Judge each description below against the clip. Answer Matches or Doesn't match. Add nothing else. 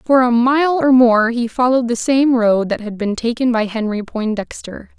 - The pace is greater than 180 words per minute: Matches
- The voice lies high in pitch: Matches